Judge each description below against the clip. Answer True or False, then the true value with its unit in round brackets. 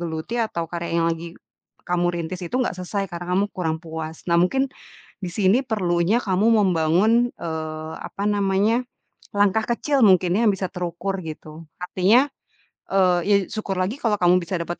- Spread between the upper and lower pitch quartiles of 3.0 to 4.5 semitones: True (3.5 semitones)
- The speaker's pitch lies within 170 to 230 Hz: True (185 Hz)